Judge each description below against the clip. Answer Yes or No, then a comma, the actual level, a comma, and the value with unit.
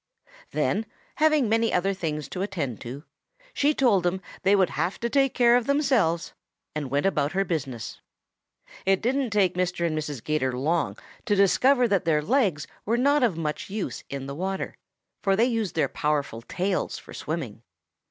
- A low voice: No, high, 190 Hz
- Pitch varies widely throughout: Yes, wide, 7.2 semitones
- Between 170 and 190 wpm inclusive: Yes, average, 175 wpm